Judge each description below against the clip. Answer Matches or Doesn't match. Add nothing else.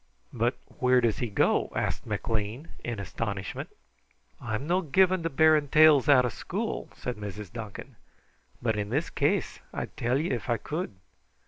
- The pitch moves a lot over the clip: Matches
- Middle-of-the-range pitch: Doesn't match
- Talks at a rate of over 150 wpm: Matches